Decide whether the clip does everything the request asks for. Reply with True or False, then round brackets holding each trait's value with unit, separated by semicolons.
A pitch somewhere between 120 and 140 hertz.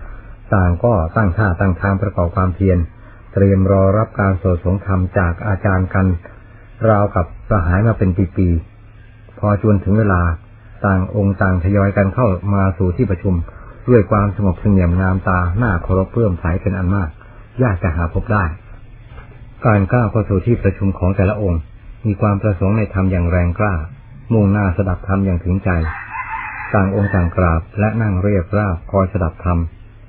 False (100 Hz)